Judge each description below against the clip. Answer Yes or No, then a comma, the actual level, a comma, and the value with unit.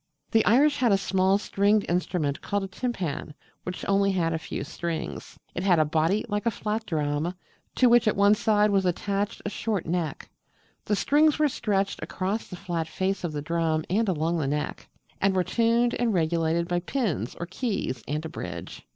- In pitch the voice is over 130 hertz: Yes, high, 190 Hz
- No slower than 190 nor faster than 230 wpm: Yes, average, 195 wpm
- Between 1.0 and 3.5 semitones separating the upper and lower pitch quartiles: No, average, 4.3 semitones